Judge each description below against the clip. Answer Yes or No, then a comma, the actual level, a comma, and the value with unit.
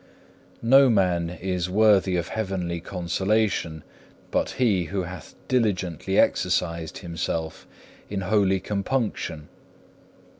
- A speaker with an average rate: No, slow, 105 wpm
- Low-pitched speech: Yes, very low, 95 Hz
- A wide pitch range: No, average, 3.3 semitones